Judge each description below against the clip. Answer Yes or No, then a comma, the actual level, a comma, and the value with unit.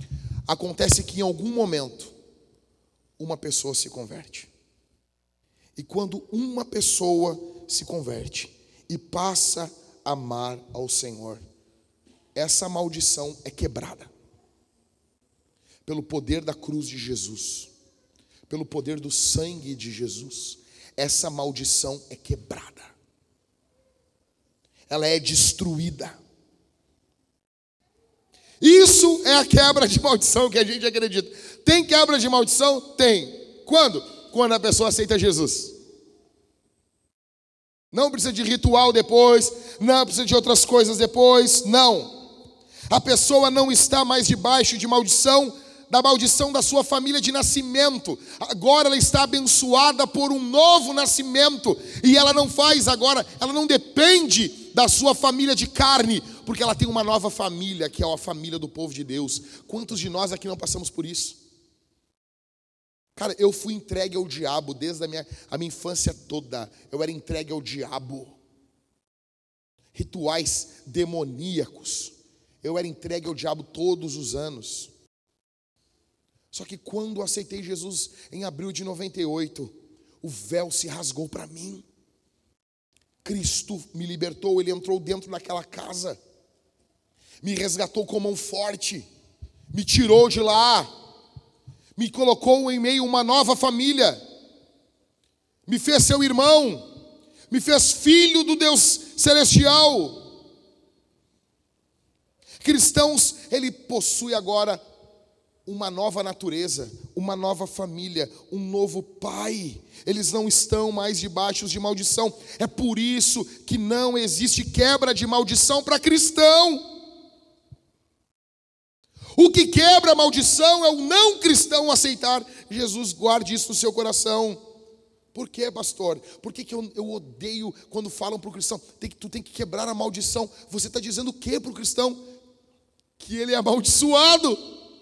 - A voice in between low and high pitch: No, high, 215 Hz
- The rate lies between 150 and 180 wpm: No, average, 130 wpm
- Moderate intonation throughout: No, wide, 7.6 semitones